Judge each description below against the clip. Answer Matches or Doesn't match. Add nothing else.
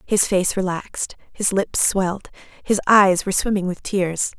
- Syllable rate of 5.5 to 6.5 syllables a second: Doesn't match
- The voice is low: Doesn't match